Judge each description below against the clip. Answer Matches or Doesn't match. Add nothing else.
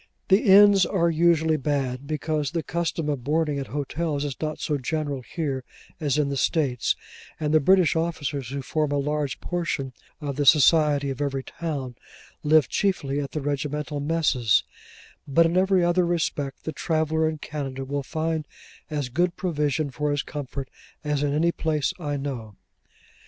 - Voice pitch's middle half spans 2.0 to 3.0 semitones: Matches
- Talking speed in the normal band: Matches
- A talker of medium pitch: Matches